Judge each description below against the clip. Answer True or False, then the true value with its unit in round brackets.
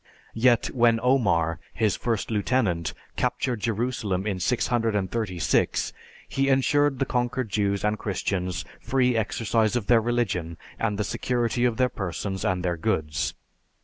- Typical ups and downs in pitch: True (4.2 semitones)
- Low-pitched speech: True (110 Hz)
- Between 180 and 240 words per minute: False (135 wpm)